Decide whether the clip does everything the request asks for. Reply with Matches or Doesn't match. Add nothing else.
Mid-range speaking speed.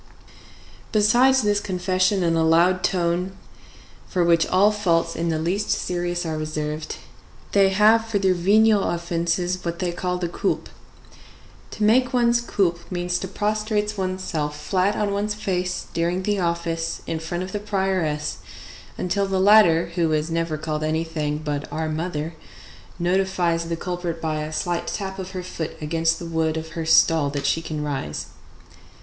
Matches